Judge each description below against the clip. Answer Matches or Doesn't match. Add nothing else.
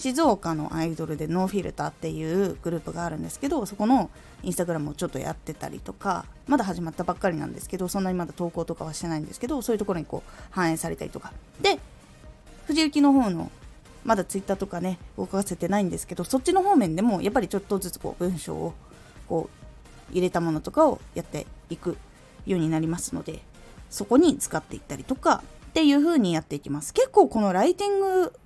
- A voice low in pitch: Doesn't match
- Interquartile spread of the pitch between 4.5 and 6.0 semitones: Doesn't match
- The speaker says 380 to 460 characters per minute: Matches